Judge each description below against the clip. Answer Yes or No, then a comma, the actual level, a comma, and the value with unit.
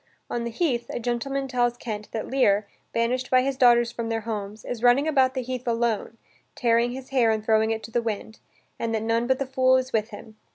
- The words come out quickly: Yes, fast, 230 wpm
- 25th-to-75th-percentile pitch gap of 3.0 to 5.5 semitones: No, narrow, 2.4 semitones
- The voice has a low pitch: No, high, 235 Hz